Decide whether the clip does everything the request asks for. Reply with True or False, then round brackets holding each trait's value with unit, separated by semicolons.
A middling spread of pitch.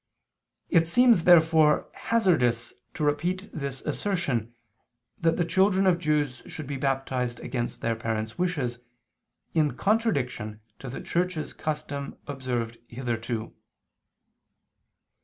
False (5.9 semitones)